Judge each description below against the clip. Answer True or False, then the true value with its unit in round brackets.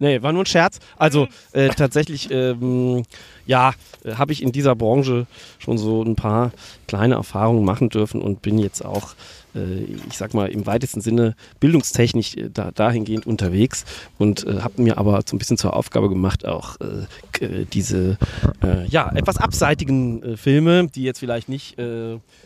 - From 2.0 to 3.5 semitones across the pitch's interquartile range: False (4.3 semitones)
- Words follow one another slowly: False (175 wpm)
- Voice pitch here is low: True (115 Hz)